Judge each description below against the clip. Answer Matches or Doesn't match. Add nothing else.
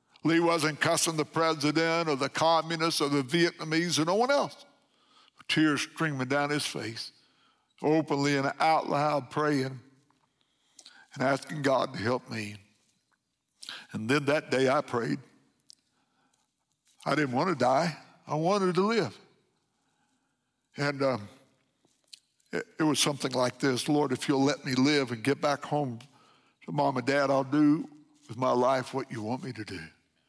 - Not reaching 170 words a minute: Matches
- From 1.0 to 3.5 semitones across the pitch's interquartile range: Matches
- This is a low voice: Doesn't match